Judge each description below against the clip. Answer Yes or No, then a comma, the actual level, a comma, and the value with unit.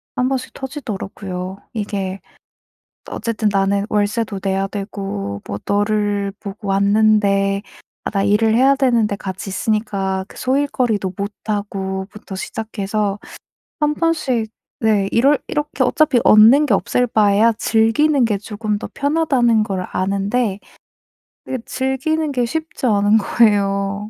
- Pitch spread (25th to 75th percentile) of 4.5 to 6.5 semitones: No, average, 3.7 semitones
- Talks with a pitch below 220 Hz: Yes, high, 210 Hz